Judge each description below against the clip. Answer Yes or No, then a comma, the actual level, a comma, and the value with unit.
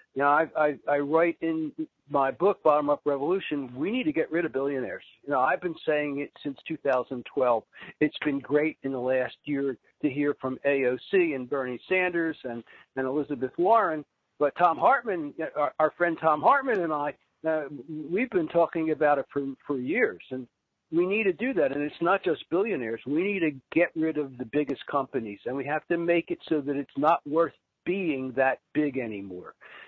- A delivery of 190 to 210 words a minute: Yes, average, 200 wpm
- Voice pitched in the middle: Yes, medium, 150 Hz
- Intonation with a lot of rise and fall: No, average, 3.4 semitones